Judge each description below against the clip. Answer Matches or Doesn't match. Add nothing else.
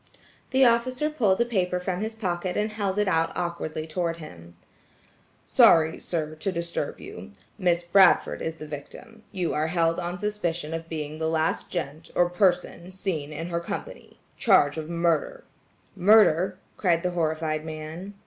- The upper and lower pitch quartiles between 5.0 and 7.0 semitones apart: Doesn't match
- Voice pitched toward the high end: Doesn't match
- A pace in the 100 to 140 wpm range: Doesn't match